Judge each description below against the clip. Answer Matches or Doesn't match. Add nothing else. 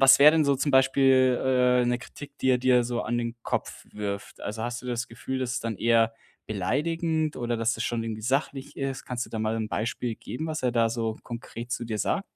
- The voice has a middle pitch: Doesn't match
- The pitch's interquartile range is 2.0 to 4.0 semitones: Matches